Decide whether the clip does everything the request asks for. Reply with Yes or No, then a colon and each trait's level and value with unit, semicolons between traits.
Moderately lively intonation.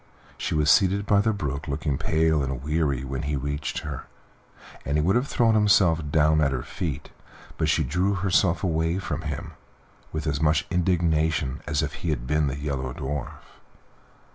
Yes: average, 3.5 semitones